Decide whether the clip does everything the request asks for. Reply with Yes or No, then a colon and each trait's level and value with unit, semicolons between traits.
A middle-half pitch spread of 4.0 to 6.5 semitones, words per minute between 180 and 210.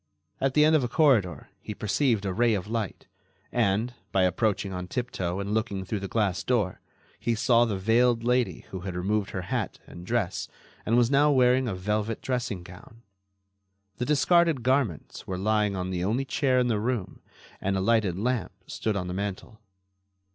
Yes: average, 4.4 semitones; average, 185 wpm